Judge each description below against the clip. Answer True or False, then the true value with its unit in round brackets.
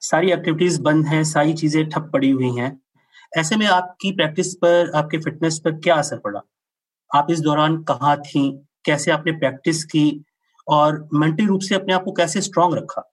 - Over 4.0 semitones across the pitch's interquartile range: False (2.7 semitones)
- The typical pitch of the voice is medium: True (160 Hz)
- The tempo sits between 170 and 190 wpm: True (185 wpm)